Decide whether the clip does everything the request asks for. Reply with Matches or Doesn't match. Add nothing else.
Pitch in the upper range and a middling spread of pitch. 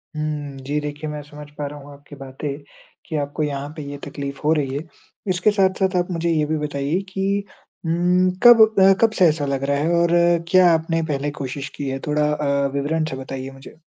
Doesn't match